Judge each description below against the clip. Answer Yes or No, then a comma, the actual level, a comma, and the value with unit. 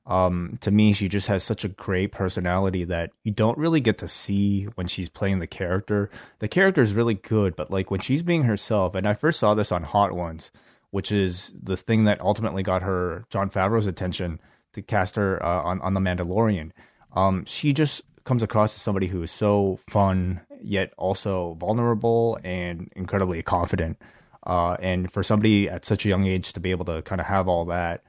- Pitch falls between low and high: No, very low, 95 Hz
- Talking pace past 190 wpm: Yes, fast, 205 wpm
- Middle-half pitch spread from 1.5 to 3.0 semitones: Yes, average, 2.7 semitones